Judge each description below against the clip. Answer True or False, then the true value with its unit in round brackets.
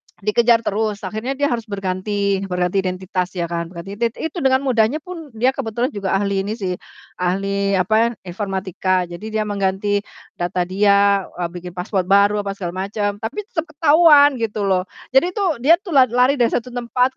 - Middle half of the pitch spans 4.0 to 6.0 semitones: True (4.5 semitones)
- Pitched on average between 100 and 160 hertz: False (205 Hz)